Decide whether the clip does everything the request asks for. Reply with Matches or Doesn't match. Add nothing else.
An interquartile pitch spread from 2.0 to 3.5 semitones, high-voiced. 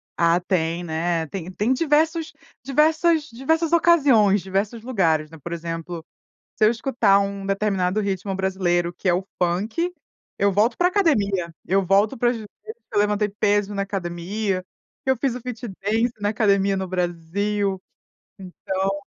Doesn't match